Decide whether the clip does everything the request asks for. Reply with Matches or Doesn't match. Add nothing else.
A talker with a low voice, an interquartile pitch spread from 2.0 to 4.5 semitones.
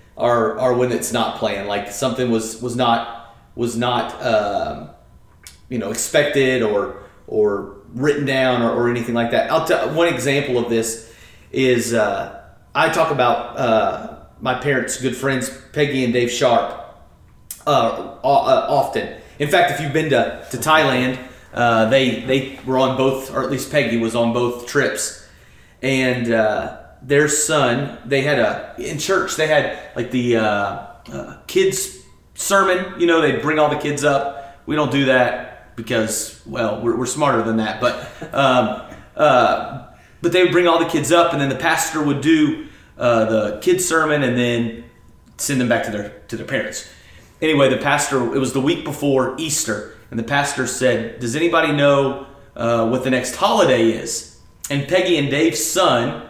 Matches